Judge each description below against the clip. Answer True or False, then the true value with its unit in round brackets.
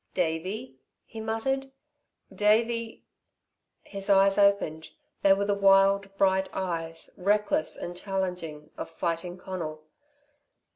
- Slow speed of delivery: True (110 wpm)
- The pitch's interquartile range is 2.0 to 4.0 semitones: True (2.9 semitones)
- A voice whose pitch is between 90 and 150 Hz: False (195 Hz)